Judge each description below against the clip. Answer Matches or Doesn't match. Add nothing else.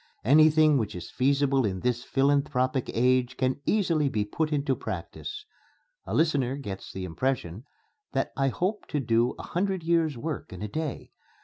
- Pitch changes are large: Doesn't match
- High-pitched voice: Doesn't match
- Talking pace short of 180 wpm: Matches